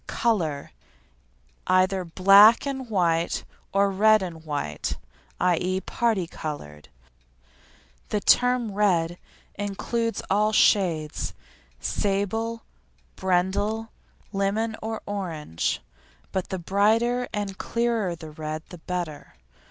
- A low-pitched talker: No, high, 195 Hz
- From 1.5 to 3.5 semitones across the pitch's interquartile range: No, average, 4.2 semitones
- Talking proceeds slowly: Yes, slow, 95 wpm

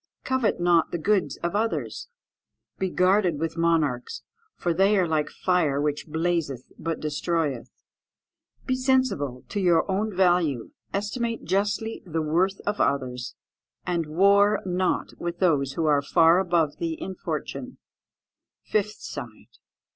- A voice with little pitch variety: No, average, 4.4 semitones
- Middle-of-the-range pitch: Yes, medium, 175 Hz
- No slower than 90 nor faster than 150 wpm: Yes, slow, 135 wpm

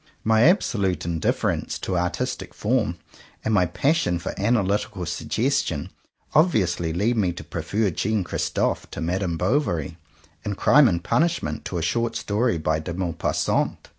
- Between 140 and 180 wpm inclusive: Yes, average, 155 wpm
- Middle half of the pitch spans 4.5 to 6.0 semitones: Yes, average, 5.2 semitones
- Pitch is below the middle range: Yes, low, 100 Hz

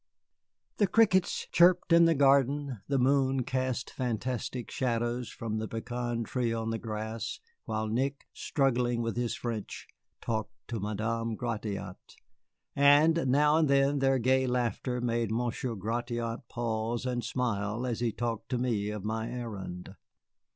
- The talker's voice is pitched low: Yes, low, 120 Hz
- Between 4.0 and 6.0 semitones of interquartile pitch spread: No, average, 2.7 semitones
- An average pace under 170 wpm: Yes, average, 145 wpm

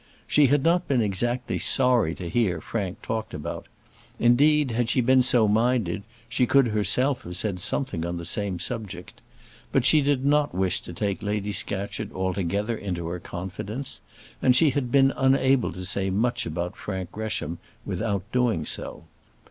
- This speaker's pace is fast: No, average, 165 wpm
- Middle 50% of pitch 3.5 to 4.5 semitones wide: No, wide, 5.4 semitones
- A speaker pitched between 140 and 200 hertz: No, low, 110 Hz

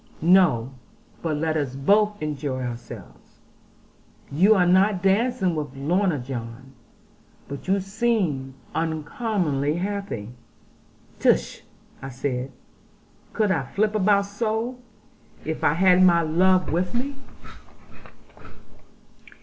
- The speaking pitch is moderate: Yes, medium, 175 Hz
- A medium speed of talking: No, slow, 105 wpm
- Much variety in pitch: Yes, wide, 6.3 semitones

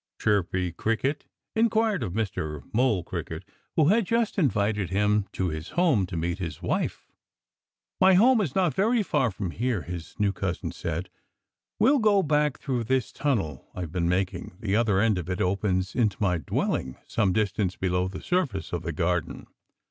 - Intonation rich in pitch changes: Yes, wide, 7.9 semitones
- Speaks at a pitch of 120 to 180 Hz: No, low, 100 Hz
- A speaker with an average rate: Yes, average, 170 wpm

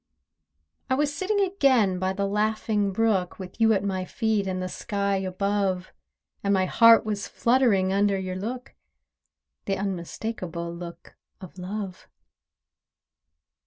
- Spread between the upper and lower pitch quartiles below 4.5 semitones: Yes, average, 2.9 semitones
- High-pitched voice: Yes, high, 200 Hz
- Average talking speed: No, slow, 130 wpm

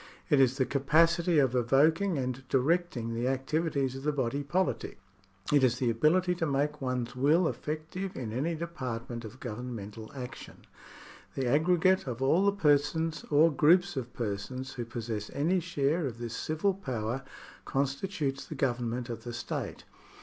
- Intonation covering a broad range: No, average, 4.8 semitones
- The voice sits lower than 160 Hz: Yes, low, 135 Hz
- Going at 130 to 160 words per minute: Yes, average, 155 wpm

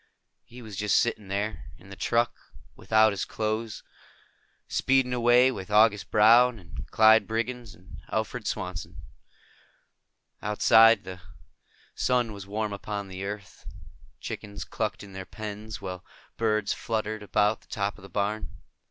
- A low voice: Yes, low, 105 Hz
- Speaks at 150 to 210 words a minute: No, average, 140 wpm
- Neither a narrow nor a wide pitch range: No, narrow, 2.1 semitones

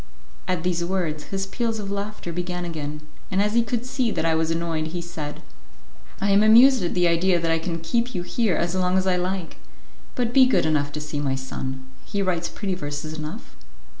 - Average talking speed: No, fast, 215 wpm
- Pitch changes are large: No, average, 3.8 semitones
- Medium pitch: Yes, medium, 180 Hz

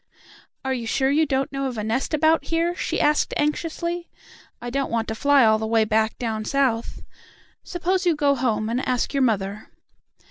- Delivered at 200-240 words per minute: No, average, 190 wpm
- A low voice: No, very high, 265 Hz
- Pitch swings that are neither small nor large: Yes, average, 5.0 semitones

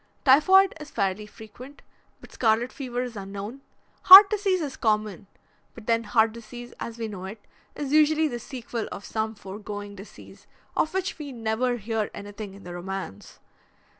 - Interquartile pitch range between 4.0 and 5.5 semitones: Yes, average, 4.6 semitones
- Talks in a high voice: Yes, high, 225 Hz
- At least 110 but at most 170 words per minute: Yes, average, 165 wpm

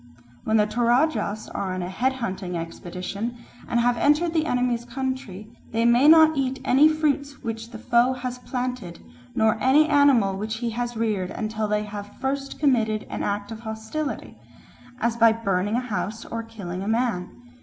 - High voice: Yes, high, 230 Hz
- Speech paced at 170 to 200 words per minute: Yes, average, 175 wpm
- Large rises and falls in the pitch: No, average, 3.6 semitones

